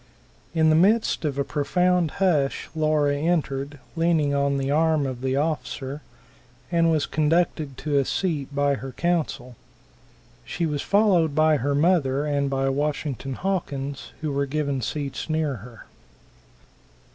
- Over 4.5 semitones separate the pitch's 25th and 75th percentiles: No, average, 2.8 semitones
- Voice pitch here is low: No, medium, 145 Hz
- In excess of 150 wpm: No, average, 145 wpm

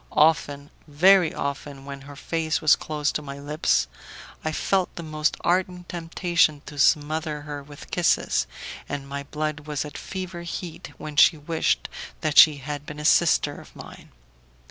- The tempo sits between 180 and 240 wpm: No, average, 165 wpm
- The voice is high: No, medium, 150 Hz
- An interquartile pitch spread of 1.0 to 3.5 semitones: Yes, narrow, 2.4 semitones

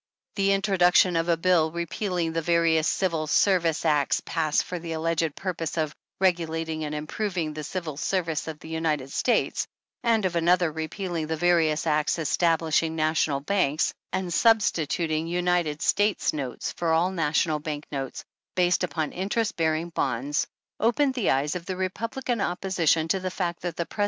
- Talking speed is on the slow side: No, average, 165 wpm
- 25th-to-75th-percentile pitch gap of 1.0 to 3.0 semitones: Yes, average, 2.7 semitones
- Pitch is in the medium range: Yes, medium, 165 Hz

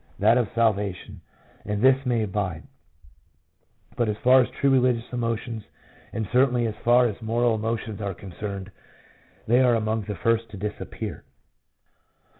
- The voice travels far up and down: No, average, 2.8 semitones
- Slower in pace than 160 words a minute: Yes, average, 145 wpm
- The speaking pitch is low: Yes, low, 115 Hz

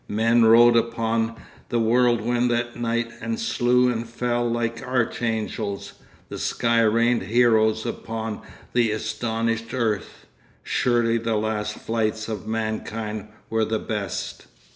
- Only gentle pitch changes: Yes, narrow, 1.3 semitones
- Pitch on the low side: Yes, low, 115 Hz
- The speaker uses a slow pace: Yes, slow, 120 wpm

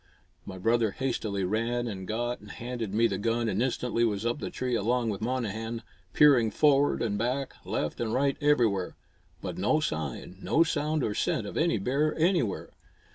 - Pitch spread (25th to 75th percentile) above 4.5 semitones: No, average, 3.8 semitones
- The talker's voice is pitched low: Yes, low, 115 Hz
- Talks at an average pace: Yes, average, 180 wpm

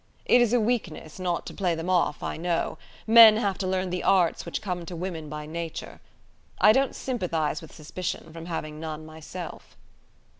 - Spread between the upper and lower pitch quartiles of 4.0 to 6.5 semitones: No, average, 3.4 semitones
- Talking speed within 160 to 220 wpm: Yes, average, 185 wpm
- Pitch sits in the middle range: Yes, medium, 175 Hz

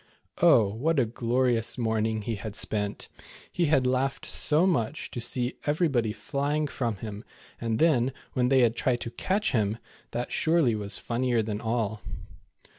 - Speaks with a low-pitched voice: Yes, low, 120 Hz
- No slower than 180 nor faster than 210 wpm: No, average, 170 wpm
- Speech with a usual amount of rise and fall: Yes, average, 3.8 semitones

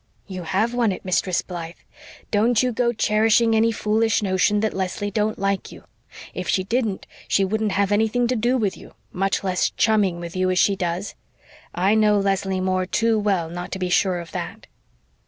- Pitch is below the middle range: No, high, 200 Hz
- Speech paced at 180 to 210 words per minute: Yes, average, 190 wpm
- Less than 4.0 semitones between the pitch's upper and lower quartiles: Yes, average, 2.9 semitones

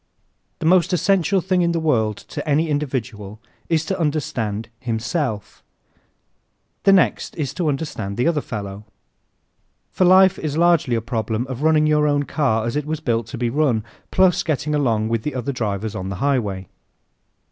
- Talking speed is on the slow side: No, average, 175 wpm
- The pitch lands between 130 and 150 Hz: Yes, medium, 140 Hz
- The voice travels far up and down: Yes, wide, 6.1 semitones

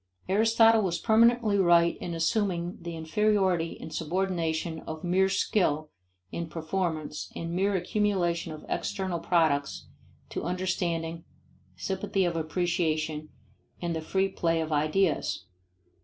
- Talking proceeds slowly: Yes, slow, 120 wpm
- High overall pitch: No, medium, 175 Hz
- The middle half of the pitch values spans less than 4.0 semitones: Yes, average, 3.0 semitones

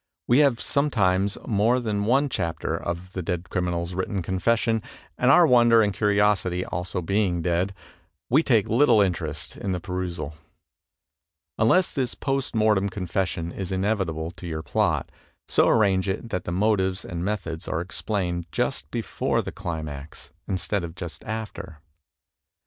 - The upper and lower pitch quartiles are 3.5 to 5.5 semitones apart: Yes, average, 4.0 semitones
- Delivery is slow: No, average, 150 wpm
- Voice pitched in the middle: No, very low, 95 Hz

